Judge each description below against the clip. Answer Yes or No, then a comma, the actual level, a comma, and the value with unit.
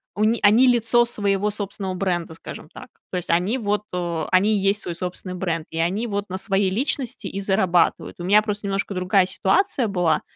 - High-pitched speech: Yes, high, 195 Hz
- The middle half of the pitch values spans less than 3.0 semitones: Yes, narrow, 2.6 semitones